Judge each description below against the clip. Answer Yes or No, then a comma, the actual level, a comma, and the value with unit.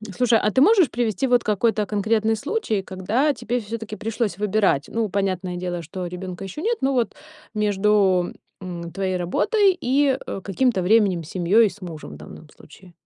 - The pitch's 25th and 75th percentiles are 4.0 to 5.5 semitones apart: Yes, average, 4.4 semitones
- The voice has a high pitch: Yes, high, 210 Hz